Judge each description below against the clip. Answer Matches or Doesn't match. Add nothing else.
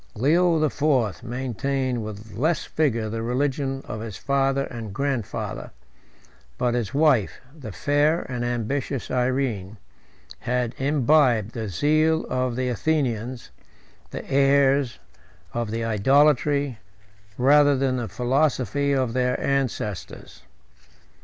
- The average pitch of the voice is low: Matches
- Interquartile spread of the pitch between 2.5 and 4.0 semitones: Matches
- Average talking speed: Doesn't match